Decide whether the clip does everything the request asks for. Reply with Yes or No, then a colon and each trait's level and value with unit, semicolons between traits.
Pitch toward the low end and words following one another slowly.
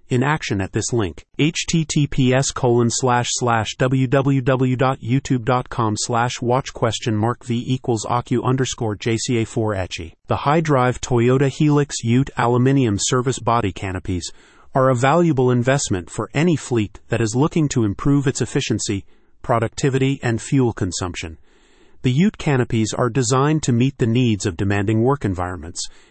Yes: low, 125 Hz; slow, 130 wpm